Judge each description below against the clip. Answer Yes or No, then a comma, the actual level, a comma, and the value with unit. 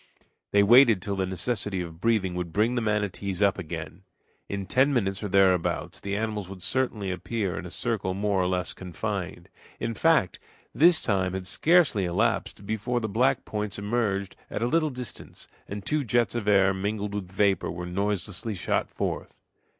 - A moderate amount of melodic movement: Yes, average, 3.5 semitones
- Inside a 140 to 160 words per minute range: No, average, 175 wpm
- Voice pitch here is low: Yes, low, 100 Hz